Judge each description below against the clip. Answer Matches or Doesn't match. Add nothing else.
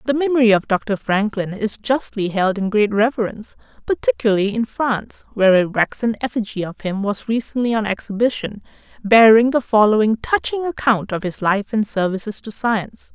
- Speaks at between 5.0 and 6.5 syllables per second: Matches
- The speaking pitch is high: Matches